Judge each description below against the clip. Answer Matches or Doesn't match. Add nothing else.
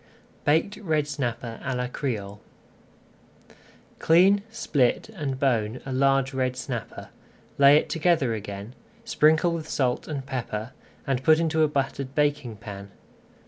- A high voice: Doesn't match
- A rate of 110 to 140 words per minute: Matches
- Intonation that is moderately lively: Matches